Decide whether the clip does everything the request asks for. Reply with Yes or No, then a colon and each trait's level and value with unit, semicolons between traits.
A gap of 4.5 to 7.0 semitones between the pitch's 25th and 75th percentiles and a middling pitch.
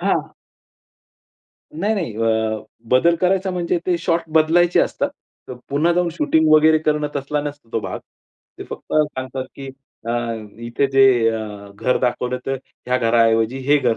Yes: average, 5.2 semitones; medium, 145 Hz